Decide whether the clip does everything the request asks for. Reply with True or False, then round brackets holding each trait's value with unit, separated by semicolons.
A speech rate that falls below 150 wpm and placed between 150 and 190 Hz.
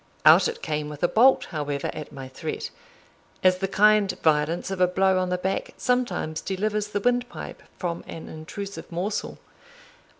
False (165 wpm; 185 Hz)